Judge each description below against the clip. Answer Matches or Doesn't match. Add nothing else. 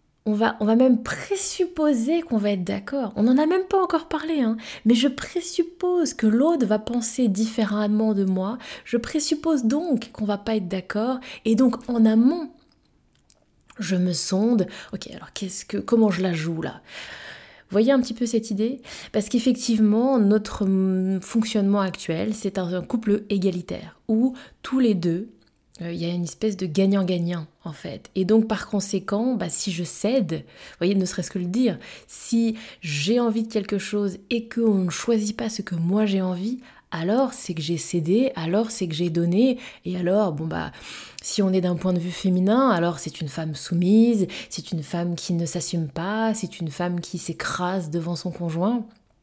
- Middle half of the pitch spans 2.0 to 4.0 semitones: Doesn't match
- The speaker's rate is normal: Matches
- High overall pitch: Matches